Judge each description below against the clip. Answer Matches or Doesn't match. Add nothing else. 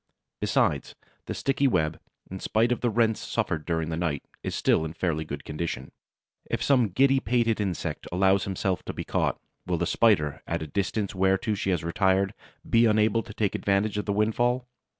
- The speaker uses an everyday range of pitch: Matches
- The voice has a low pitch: Matches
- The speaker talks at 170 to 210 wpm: Matches